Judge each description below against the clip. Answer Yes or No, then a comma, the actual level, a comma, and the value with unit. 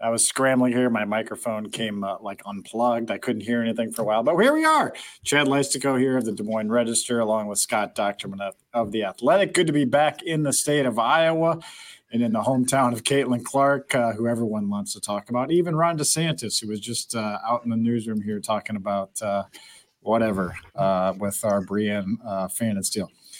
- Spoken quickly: Yes, fast, 215 wpm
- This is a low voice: Yes, low, 115 Hz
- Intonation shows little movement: No, average, 4.4 semitones